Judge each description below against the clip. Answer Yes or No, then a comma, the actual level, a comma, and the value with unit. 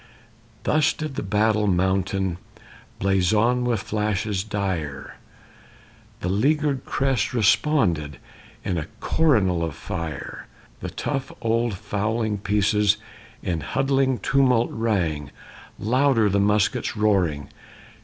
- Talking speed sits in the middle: No, slow, 105 wpm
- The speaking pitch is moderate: No, low, 105 Hz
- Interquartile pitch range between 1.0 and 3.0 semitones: No, average, 4.4 semitones